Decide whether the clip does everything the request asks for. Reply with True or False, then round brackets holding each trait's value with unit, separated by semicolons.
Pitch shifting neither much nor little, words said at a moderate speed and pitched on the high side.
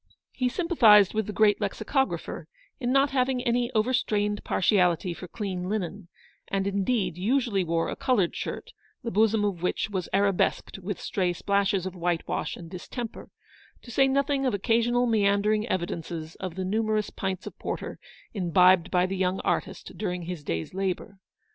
True (4.0 semitones; 160 wpm; 200 Hz)